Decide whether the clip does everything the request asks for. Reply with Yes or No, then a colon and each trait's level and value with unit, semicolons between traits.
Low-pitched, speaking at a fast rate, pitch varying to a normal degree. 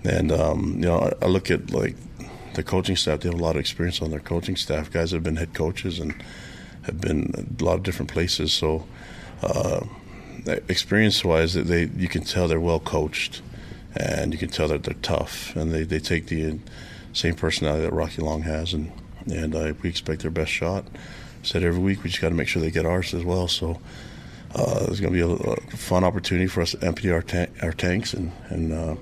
No: very low, 85 Hz; fast, 225 wpm; narrow, 2.3 semitones